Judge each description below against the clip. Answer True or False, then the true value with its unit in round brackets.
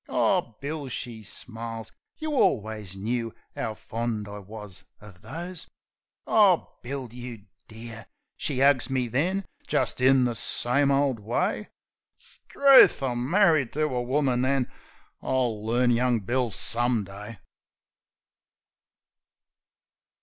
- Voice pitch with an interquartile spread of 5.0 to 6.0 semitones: False (3.7 semitones)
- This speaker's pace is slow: True (120 wpm)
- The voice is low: True (125 Hz)